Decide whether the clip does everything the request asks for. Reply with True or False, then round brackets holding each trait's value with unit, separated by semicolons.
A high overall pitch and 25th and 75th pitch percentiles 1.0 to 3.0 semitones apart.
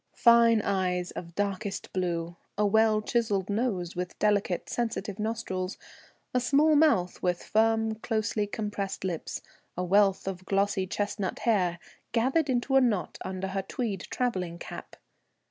False (205 Hz; 3.4 semitones)